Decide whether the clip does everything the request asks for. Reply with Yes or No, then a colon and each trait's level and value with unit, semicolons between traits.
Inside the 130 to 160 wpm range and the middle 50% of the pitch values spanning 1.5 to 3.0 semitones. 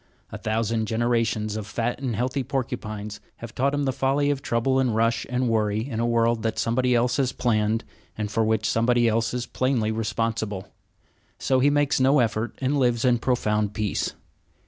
No: average, 185 wpm; average, 2.7 semitones